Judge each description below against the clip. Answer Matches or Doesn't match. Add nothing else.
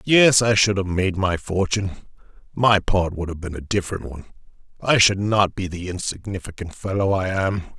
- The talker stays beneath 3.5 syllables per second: Doesn't match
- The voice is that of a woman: Doesn't match